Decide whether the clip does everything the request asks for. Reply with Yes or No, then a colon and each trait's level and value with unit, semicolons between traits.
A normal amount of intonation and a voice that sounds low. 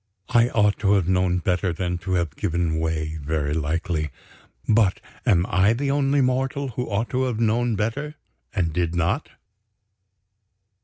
No: wide, 6.0 semitones; very low, 95 Hz